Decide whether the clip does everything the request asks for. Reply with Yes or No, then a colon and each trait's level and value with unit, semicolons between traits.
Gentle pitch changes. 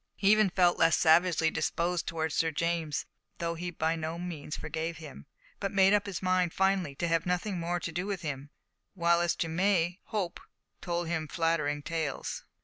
Yes: narrow, 2.0 semitones